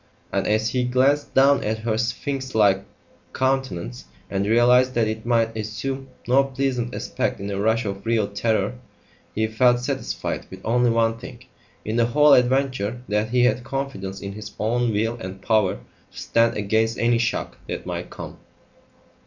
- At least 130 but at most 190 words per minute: Yes, average, 170 wpm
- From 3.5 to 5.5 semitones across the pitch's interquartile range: No, average, 2.8 semitones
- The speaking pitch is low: Yes, low, 115 Hz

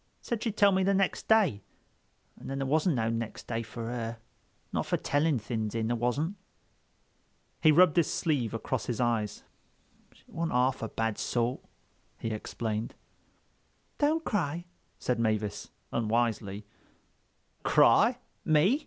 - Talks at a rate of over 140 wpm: No, slow, 135 wpm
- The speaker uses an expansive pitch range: Yes, wide, 6.3 semitones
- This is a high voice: No, low, 120 Hz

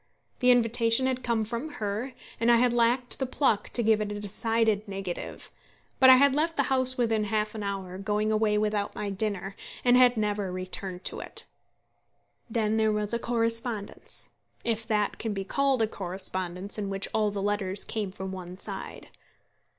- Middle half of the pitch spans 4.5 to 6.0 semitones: No, average, 2.9 semitones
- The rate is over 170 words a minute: Yes, average, 180 wpm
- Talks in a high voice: Yes, high, 215 Hz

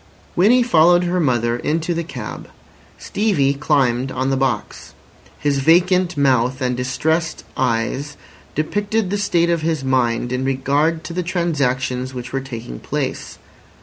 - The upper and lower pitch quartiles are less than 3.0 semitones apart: No, average, 5.0 semitones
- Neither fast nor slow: Yes, average, 145 wpm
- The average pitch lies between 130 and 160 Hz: Yes, medium, 140 Hz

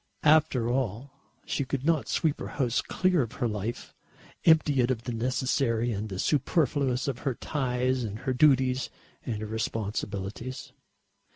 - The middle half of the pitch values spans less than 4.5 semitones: Yes, average, 3.4 semitones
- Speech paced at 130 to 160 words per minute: Yes, average, 155 wpm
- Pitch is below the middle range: Yes, low, 125 Hz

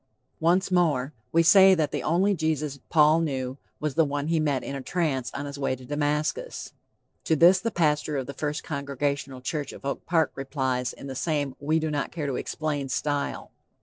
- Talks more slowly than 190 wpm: No, average, 200 wpm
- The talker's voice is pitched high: No, medium, 150 Hz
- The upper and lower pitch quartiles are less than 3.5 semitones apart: Yes, average, 2.7 semitones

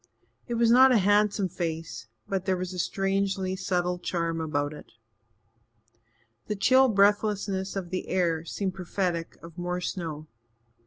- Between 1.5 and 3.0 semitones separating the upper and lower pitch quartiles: Yes, average, 2.7 semitones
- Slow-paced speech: No, average, 145 wpm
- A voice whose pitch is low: No, medium, 185 Hz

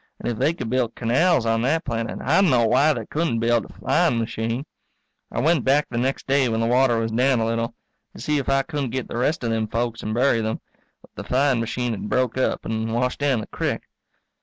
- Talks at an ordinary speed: No, fast, 235 wpm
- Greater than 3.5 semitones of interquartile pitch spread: No, average, 3.1 semitones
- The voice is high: No, low, 120 Hz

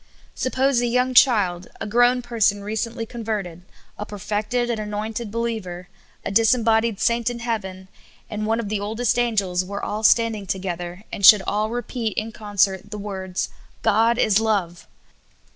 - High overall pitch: Yes, high, 215 Hz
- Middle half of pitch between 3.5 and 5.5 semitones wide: No, average, 2.7 semitones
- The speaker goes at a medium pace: Yes, average, 165 wpm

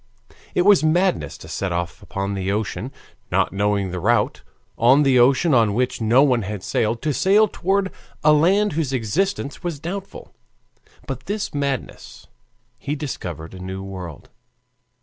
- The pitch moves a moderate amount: No, wide, 8.5 semitones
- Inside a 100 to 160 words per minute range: Yes, average, 155 wpm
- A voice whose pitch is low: Yes, low, 125 Hz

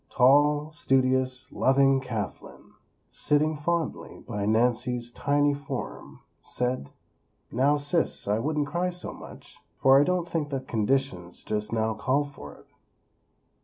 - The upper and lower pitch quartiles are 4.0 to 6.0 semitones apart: No, average, 3.5 semitones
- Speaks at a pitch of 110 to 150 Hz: Yes, low, 135 Hz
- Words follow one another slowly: Yes, slow, 130 wpm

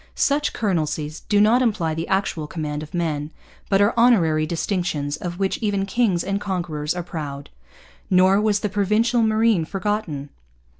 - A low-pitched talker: No, medium, 185 Hz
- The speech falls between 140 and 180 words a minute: Yes, average, 155 wpm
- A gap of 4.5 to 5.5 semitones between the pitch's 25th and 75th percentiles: Yes, average, 5.0 semitones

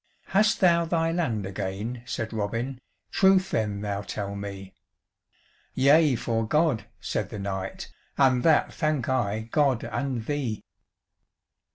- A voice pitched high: No, low, 120 Hz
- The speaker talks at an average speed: No, slow, 130 wpm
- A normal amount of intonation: No, wide, 6.6 semitones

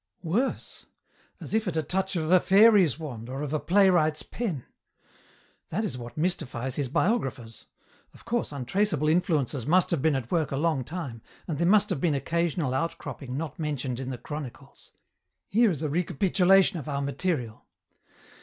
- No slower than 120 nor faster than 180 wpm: Yes, average, 170 wpm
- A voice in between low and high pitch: Yes, medium, 155 Hz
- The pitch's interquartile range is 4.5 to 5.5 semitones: Yes, average, 5.2 semitones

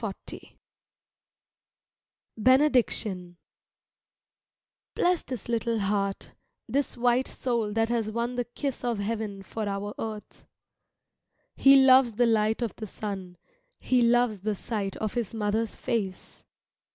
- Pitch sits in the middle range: No, high, 225 Hz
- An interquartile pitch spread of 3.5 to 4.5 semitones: No, average, 2.8 semitones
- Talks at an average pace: No, slow, 120 wpm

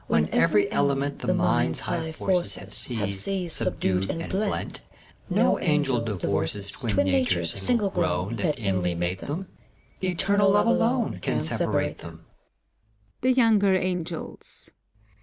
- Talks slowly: Yes, slow, 115 wpm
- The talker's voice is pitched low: Yes, low, 125 Hz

